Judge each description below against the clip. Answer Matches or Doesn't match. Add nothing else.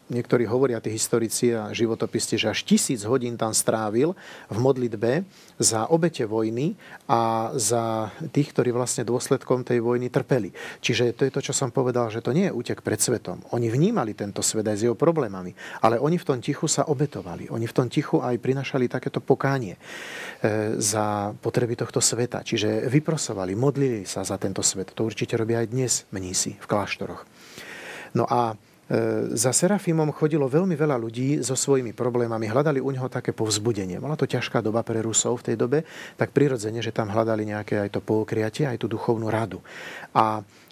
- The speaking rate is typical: Doesn't match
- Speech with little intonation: Doesn't match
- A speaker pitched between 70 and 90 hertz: Doesn't match